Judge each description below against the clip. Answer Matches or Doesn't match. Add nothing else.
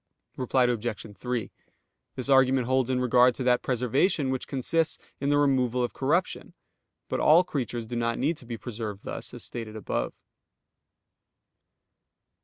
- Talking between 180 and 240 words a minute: Doesn't match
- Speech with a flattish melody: Matches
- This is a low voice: Matches